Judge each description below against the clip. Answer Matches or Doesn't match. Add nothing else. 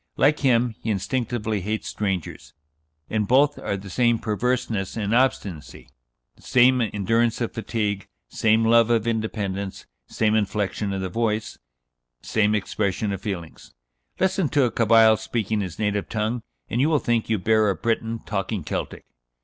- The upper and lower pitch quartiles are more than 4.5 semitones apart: Doesn't match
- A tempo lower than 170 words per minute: Matches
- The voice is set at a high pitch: Doesn't match